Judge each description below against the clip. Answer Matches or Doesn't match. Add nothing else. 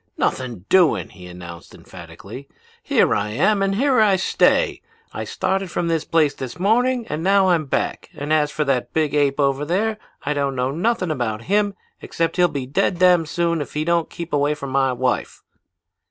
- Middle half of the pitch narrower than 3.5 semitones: Doesn't match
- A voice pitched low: Doesn't match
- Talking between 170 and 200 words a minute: Matches